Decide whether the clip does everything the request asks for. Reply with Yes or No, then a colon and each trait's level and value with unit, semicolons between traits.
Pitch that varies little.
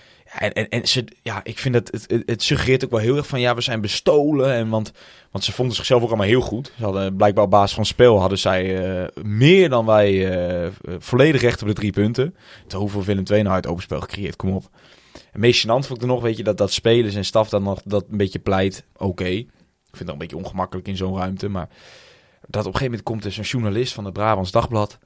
No: average, 3.6 semitones